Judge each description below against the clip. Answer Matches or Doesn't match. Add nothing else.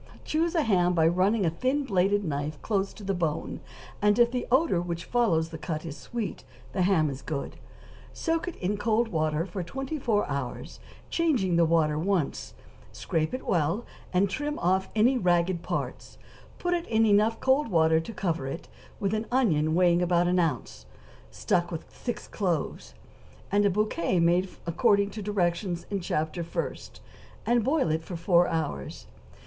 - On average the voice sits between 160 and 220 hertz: Matches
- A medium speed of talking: Matches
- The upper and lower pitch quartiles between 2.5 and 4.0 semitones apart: Doesn't match